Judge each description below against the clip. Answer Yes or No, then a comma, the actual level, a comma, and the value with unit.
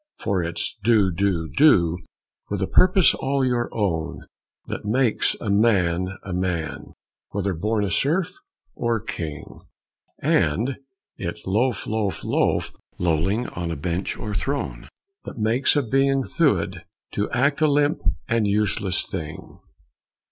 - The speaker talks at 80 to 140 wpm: Yes, slow, 135 wpm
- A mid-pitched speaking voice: No, low, 105 Hz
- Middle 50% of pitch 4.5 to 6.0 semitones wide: Yes, wide, 5.5 semitones